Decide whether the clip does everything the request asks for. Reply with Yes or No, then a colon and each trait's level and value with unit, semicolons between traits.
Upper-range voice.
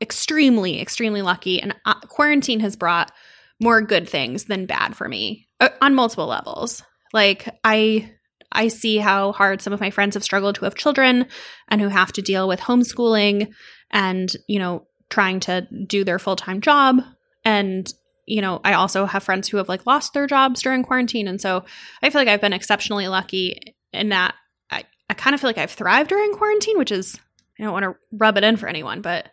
Yes: high, 210 Hz